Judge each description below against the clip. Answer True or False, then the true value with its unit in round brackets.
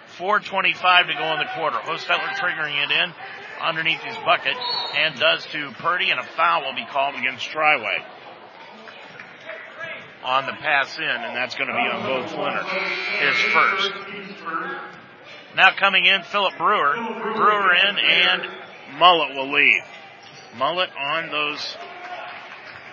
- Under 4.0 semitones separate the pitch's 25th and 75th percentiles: True (2.6 semitones)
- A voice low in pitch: False (195 Hz)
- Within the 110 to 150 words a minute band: True (140 wpm)